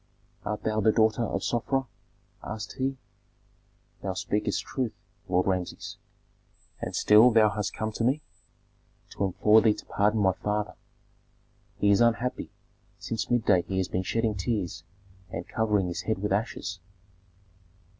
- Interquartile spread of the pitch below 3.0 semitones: Yes, narrow, 2.6 semitones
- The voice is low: Yes, low, 105 Hz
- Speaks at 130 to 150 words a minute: Yes, average, 145 wpm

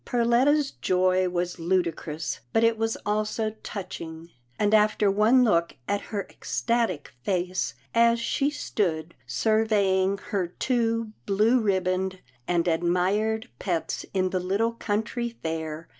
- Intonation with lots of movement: No, average, 4.0 semitones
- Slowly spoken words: Yes, slow, 125 wpm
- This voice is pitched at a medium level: No, high, 200 Hz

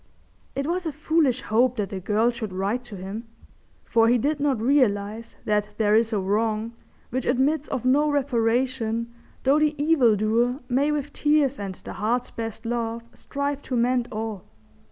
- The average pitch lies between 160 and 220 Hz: No, high, 240 Hz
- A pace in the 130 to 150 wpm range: No, average, 170 wpm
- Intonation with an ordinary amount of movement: Yes, average, 4.1 semitones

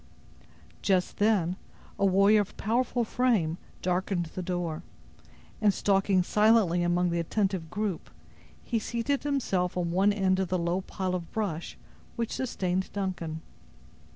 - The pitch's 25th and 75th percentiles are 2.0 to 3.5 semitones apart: Yes, average, 3.1 semitones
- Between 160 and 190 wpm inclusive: No, slow, 135 wpm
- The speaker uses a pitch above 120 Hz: Yes, high, 190 Hz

